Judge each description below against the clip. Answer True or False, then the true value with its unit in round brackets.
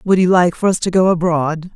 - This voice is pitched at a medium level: True (175 Hz)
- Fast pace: True (275 wpm)